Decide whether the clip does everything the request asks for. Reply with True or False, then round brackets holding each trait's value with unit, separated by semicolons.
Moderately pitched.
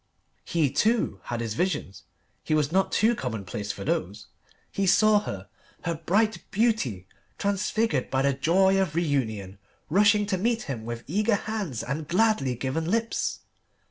True (165 Hz)